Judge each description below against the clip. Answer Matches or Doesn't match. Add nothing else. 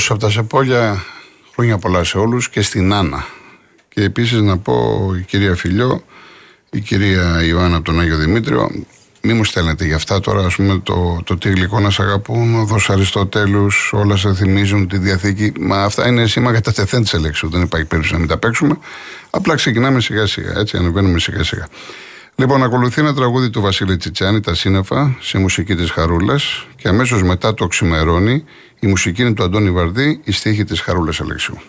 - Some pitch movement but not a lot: Matches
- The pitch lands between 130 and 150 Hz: Doesn't match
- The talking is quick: Matches